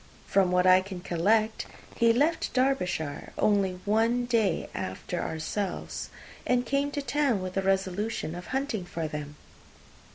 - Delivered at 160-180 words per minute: No, average, 140 wpm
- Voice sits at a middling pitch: No, high, 200 Hz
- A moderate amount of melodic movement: Yes, average, 5.0 semitones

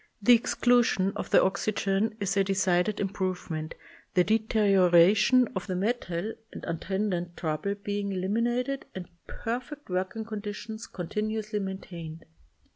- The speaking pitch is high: Yes, high, 200 Hz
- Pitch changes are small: No, average, 3.0 semitones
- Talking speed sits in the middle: No, slow, 125 wpm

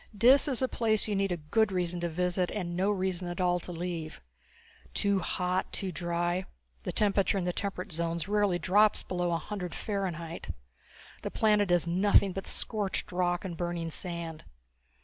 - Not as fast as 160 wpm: No, average, 175 wpm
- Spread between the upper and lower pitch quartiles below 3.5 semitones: Yes, narrow, 2.6 semitones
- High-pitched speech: No, medium, 180 Hz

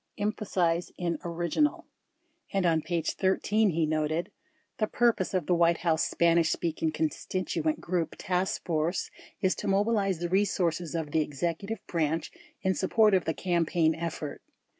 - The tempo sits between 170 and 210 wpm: No, average, 155 wpm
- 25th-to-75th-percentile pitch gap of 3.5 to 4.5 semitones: No, average, 2.8 semitones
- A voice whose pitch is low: No, medium, 170 Hz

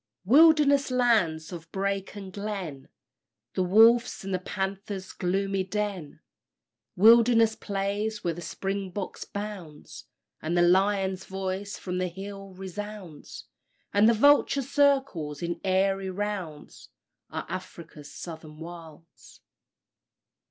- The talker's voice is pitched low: No, high, 195 Hz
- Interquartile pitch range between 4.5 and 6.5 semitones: No, average, 3.0 semitones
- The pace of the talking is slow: Yes, slow, 110 wpm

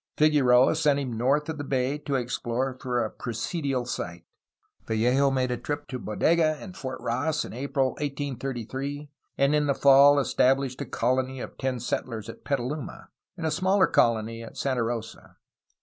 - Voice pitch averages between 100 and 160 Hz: Yes, low, 135 Hz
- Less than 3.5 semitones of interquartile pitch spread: Yes, average, 2.9 semitones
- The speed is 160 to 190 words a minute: Yes, average, 165 wpm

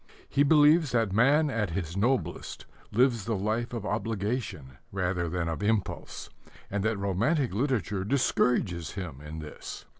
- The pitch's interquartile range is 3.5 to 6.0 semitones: Yes, average, 5.2 semitones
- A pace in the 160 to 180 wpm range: No, average, 145 wpm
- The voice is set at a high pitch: No, low, 105 Hz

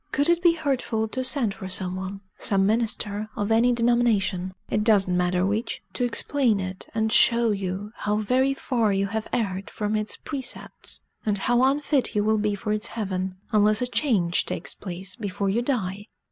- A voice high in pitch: Yes, high, 215 Hz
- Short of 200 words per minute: Yes, average, 190 wpm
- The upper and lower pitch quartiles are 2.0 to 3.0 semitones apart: No, average, 3.6 semitones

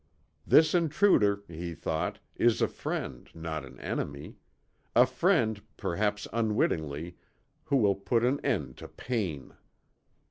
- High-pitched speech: No, low, 100 Hz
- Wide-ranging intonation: Yes, wide, 6.9 semitones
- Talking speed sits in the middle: No, slow, 120 wpm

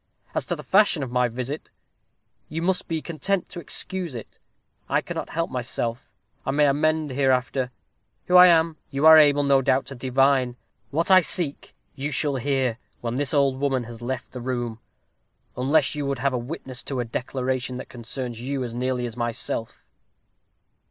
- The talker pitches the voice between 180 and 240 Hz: No, low, 135 Hz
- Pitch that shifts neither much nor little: Yes, average, 3.2 semitones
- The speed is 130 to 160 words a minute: No, average, 180 wpm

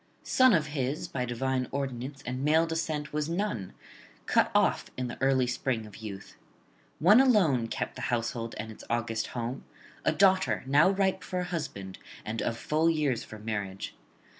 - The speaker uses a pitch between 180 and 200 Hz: No, low, 130 Hz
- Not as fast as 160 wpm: No, average, 170 wpm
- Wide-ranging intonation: Yes, wide, 5.7 semitones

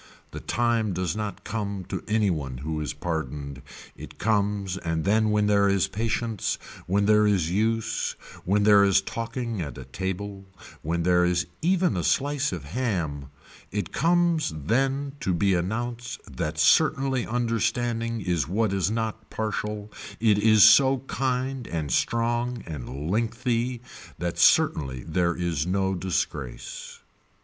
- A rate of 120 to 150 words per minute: Yes, average, 145 wpm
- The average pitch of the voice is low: Yes, low, 105 Hz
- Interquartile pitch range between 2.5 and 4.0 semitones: No, average, 5.0 semitones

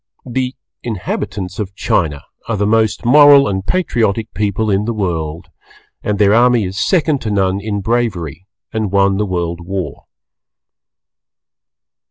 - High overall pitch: No, low, 105 Hz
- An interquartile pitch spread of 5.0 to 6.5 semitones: No, average, 3.5 semitones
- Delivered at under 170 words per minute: Yes, average, 140 wpm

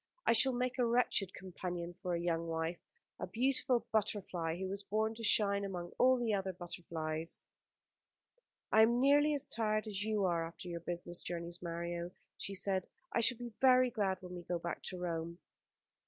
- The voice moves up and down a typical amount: Yes, average, 4.6 semitones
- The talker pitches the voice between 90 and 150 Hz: No, high, 190 Hz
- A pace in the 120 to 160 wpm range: No, average, 185 wpm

